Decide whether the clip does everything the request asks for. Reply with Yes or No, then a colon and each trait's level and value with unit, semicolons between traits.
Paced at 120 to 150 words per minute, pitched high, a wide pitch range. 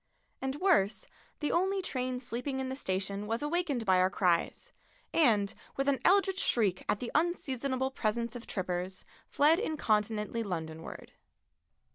Yes: average, 140 wpm; high, 245 Hz; wide, 6.4 semitones